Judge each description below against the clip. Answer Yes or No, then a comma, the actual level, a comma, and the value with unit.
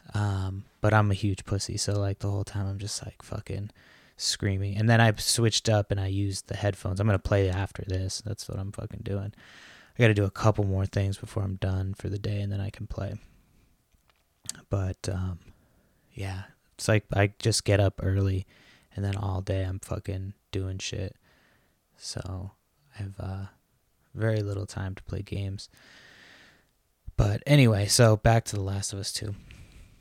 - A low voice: Yes, low, 100 Hz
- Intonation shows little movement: Yes, narrow, 1.8 semitones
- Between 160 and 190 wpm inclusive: Yes, average, 185 wpm